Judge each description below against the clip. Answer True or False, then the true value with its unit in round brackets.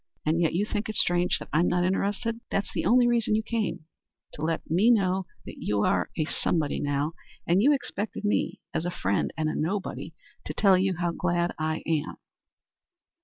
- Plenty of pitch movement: False (4.6 semitones)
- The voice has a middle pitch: True (175 Hz)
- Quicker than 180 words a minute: True (195 wpm)